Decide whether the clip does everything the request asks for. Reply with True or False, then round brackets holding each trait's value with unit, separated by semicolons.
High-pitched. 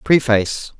False (125 Hz)